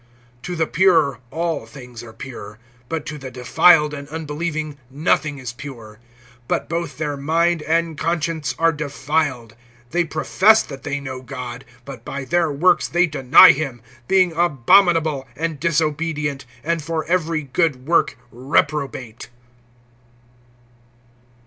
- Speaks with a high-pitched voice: No, medium, 150 Hz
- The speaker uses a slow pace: Yes, slow, 130 wpm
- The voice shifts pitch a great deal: No, average, 3.7 semitones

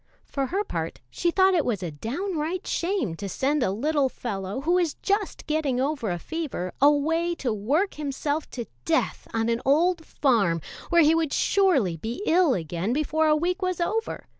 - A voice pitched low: No, very high, 300 Hz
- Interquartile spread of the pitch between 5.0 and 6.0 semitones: No, wide, 6.7 semitones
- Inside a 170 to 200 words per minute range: Yes, average, 185 wpm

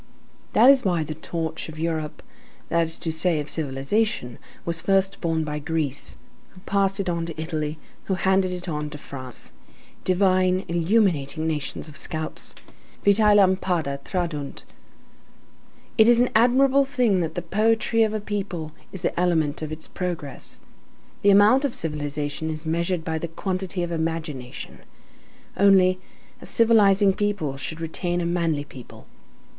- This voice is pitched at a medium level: Yes, medium, 170 Hz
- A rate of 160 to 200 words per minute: No, average, 150 wpm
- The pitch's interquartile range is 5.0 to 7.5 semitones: No, average, 3.9 semitones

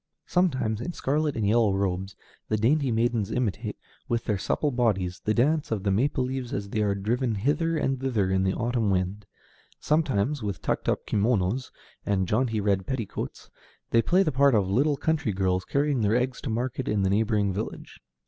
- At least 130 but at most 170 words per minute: No, average, 185 wpm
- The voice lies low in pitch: Yes, low, 115 Hz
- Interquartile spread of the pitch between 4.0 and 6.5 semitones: Yes, average, 4.9 semitones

